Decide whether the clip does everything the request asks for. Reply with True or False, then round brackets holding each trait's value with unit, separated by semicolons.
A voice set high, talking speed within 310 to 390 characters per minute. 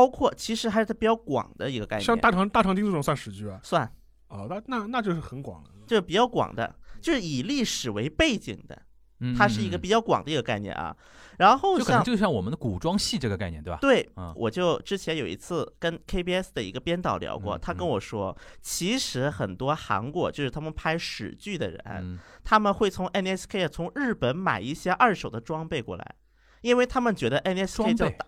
False (175 Hz; 320 characters per minute)